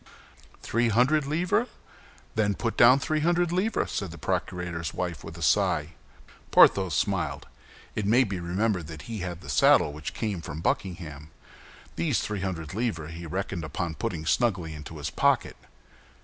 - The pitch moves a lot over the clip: Yes, wide, 6.0 semitones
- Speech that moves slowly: No, average, 160 wpm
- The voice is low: Yes, very low, 95 Hz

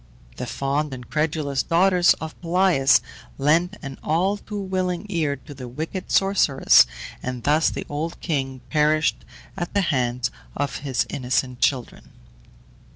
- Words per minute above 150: No, average, 140 wpm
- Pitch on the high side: No, medium, 150 Hz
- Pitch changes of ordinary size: Yes, average, 4.6 semitones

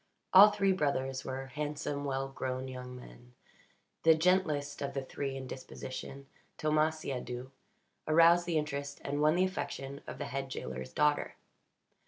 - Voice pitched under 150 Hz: Yes, medium, 140 Hz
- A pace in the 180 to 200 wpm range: No, average, 150 wpm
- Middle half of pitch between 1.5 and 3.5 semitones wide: Yes, average, 2.8 semitones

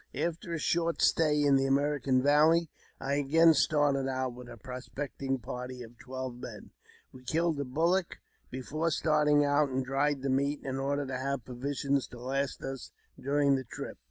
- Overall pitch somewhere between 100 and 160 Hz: Yes, medium, 140 Hz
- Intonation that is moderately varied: No, narrow, 2.2 semitones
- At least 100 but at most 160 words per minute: No, average, 170 wpm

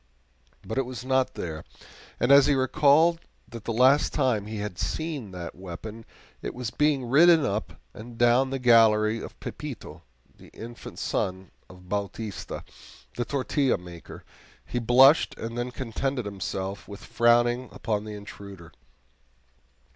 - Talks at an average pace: Yes, average, 145 wpm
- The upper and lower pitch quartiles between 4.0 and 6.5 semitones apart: Yes, average, 4.3 semitones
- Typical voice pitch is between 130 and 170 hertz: No, low, 120 Hz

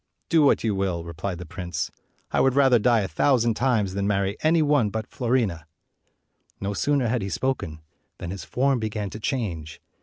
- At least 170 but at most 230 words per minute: Yes, average, 190 wpm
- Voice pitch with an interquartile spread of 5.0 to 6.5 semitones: Yes, wide, 5.5 semitones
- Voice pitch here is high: No, low, 105 Hz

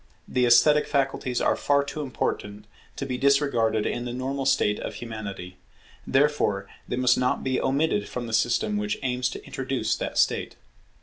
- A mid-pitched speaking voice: No, low, 125 Hz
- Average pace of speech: Yes, average, 170 wpm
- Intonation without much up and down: No, average, 3.4 semitones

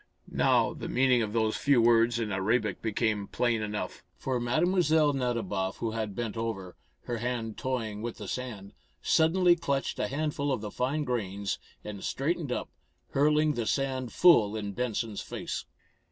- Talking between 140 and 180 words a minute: Yes, average, 160 wpm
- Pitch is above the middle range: No, low, 120 Hz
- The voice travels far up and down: No, average, 4.1 semitones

